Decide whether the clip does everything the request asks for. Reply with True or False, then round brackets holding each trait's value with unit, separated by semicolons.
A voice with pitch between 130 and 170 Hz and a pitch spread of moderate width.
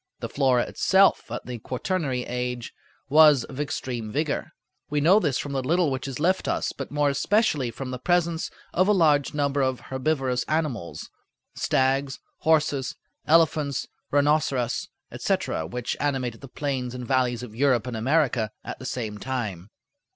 True (135 Hz; 3.4 semitones)